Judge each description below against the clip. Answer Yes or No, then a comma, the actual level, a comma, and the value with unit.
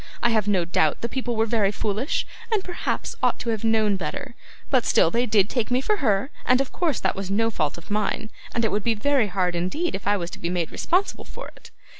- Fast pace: Yes, fast, 245 wpm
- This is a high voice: Yes, high, 220 Hz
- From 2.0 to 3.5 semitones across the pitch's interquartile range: No, average, 4.3 semitones